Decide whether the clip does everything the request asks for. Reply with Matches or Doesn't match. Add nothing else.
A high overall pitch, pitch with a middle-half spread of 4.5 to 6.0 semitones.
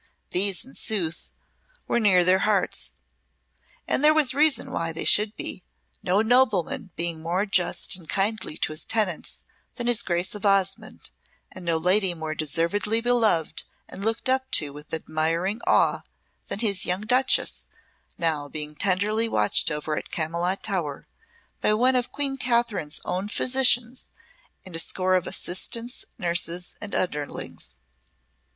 Matches